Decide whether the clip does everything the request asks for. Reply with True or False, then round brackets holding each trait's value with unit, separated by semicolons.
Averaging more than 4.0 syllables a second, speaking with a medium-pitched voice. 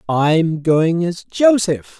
False (3.3 syllables/s; 170 Hz)